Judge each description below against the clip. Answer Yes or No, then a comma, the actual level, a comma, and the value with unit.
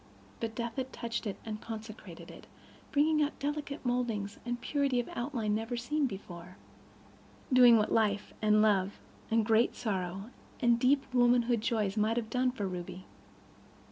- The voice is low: No, high, 230 Hz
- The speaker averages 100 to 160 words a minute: Yes, average, 150 wpm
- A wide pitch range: No, average, 2.9 semitones